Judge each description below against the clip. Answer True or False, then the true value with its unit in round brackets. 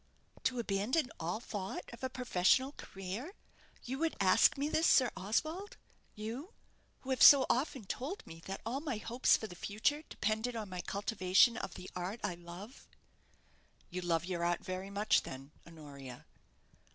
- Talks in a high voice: True (215 Hz)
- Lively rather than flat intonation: True (6.1 semitones)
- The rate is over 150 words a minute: True (165 wpm)